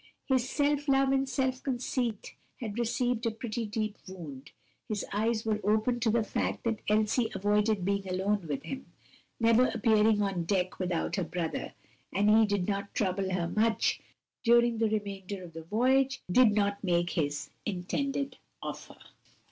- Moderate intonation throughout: Yes, average, 3.7 semitones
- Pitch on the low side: No, high, 215 Hz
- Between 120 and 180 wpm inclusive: Yes, average, 160 wpm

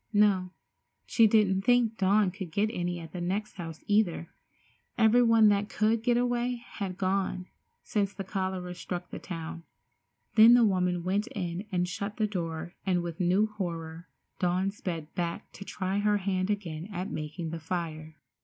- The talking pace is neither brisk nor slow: Yes, average, 165 wpm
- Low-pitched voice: No, high, 190 Hz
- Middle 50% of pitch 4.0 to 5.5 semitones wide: No, average, 3.2 semitones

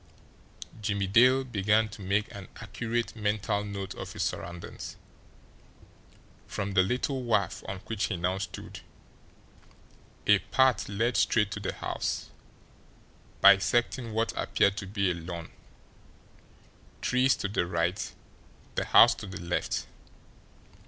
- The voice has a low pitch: Yes, low, 100 Hz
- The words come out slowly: Yes, slow, 125 wpm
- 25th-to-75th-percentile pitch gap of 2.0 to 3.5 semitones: Yes, average, 2.9 semitones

